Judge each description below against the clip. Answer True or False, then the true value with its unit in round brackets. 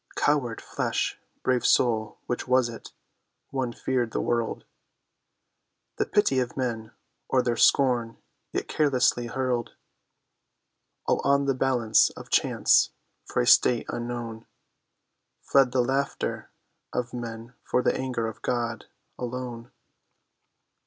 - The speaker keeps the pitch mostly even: True (1.8 semitones)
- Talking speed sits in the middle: False (120 wpm)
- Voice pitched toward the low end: True (125 Hz)